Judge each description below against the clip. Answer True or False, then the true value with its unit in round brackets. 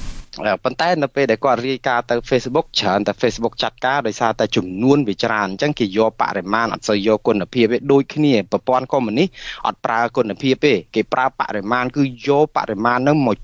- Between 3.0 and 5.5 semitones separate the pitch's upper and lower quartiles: True (4.1 semitones)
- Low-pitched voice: True (120 Hz)